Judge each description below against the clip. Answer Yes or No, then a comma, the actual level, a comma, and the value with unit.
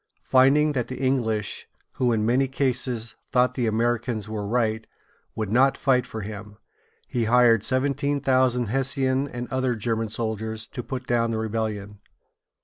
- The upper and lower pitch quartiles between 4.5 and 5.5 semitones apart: No, average, 2.8 semitones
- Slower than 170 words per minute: Yes, average, 150 wpm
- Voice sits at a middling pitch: No, low, 120 Hz